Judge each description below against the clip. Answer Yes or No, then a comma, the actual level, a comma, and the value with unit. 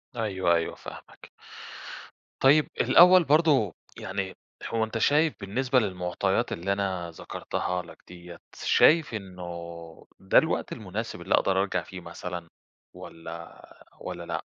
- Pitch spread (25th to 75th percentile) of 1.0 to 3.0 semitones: No, average, 5.1 semitones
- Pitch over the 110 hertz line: No, very low, 95 Hz